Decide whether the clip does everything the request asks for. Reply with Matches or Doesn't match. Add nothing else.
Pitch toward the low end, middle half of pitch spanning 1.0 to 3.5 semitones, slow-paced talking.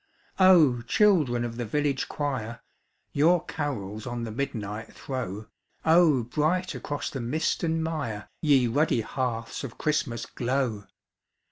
Doesn't match